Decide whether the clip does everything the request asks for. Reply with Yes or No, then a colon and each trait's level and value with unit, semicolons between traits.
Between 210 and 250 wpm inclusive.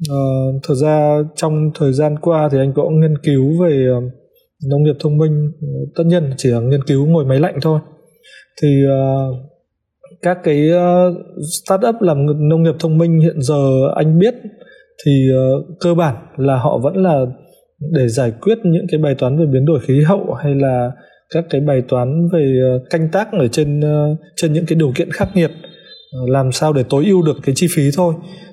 No: average, 200 wpm